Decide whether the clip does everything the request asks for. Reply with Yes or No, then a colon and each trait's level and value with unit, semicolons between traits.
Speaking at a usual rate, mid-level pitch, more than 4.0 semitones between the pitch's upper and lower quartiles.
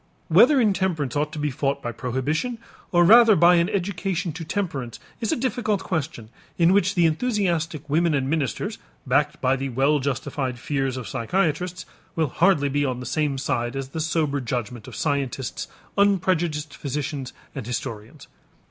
Yes: average, 165 wpm; medium, 150 Hz; average, 4.9 semitones